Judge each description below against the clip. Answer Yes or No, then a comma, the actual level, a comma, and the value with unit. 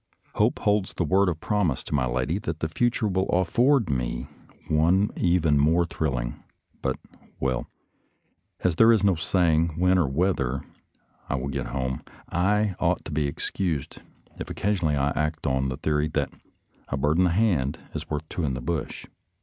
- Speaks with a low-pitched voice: Yes, very low, 80 Hz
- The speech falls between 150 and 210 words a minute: Yes, average, 185 wpm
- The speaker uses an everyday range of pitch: Yes, average, 5.0 semitones